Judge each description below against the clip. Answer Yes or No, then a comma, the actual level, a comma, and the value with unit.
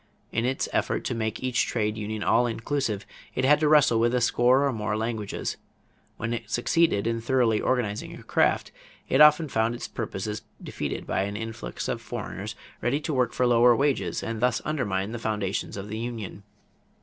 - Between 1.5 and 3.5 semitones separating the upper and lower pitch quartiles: Yes, average, 2.8 semitones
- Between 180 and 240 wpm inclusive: Yes, average, 185 wpm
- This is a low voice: Yes, low, 115 Hz